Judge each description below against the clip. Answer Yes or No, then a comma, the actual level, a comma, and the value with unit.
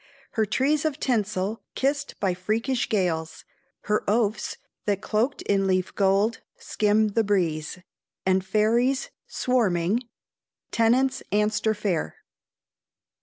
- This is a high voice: Yes, high, 210 Hz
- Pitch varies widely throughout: No, average, 3.8 semitones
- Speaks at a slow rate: Yes, slow, 115 wpm